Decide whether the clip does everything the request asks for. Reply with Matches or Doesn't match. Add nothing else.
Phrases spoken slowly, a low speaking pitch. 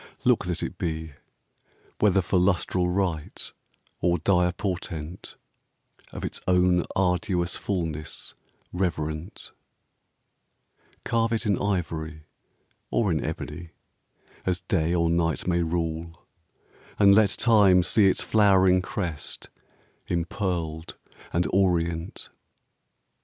Matches